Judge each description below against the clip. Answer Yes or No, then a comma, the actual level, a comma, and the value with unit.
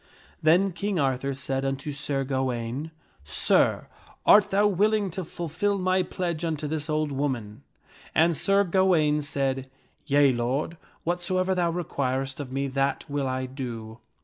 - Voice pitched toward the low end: No, medium, 145 Hz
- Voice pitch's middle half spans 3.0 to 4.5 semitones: No, average, 4.9 semitones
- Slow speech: No, average, 150 wpm